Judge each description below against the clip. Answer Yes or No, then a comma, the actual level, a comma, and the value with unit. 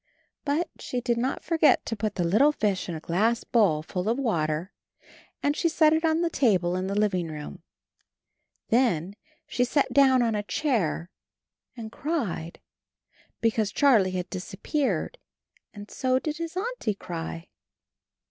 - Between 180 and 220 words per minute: No, average, 155 wpm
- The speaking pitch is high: Yes, high, 225 Hz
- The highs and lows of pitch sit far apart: Yes, wide, 7.4 semitones